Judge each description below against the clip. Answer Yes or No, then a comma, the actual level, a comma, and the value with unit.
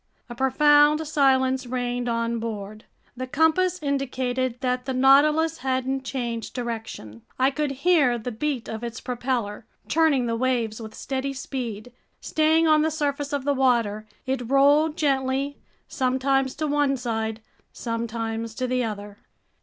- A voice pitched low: No, very high, 260 Hz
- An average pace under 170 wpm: Yes, average, 145 wpm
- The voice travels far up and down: No, average, 3.3 semitones